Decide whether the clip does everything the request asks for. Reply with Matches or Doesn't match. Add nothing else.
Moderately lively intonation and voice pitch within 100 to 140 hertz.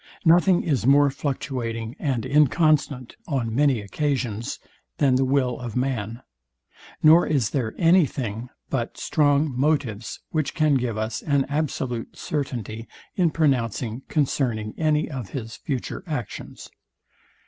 Matches